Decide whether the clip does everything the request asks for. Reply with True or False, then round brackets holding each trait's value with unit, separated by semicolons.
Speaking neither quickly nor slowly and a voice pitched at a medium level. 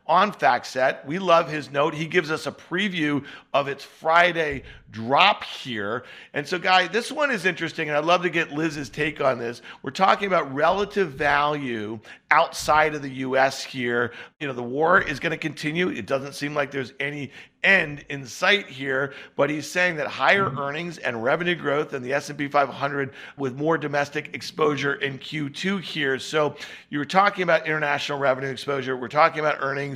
True (185 wpm; 145 Hz)